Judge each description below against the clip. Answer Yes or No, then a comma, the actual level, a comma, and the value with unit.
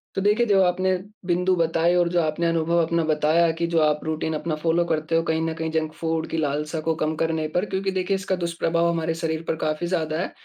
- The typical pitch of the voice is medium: Yes, medium, 165 Hz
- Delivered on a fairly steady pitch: Yes, narrow, 1.6 semitones